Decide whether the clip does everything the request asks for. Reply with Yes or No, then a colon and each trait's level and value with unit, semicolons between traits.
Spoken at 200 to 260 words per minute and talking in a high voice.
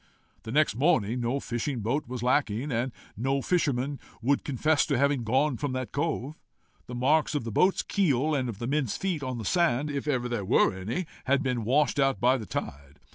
No: fast, 205 wpm; low, 130 Hz